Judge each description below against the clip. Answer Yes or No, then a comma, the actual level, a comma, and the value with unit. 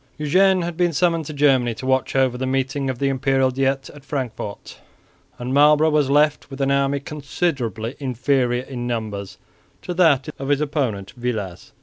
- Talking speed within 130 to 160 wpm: No, average, 170 wpm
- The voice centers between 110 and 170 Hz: Yes, low, 135 Hz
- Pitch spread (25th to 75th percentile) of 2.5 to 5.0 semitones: Yes, average, 2.9 semitones